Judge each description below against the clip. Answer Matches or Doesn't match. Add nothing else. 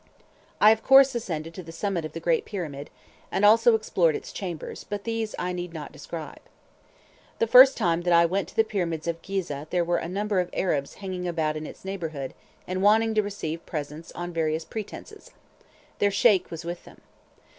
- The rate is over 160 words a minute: Matches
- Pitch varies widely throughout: Doesn't match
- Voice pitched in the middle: Matches